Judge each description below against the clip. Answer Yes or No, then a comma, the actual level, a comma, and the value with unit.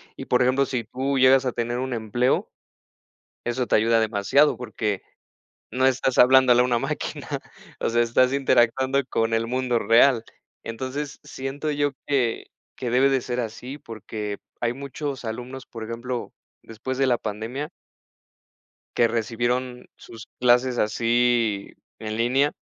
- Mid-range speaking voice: No, low, 125 Hz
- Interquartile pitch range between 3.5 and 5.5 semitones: No, narrow, 2.4 semitones